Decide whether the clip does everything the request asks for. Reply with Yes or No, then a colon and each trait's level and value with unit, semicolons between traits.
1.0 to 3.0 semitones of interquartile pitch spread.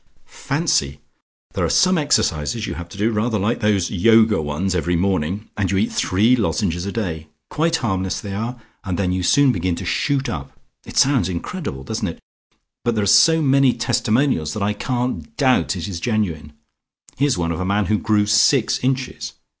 No: wide, 5.5 semitones